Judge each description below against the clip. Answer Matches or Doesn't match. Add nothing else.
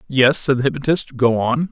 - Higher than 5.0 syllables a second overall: Matches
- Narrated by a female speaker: Doesn't match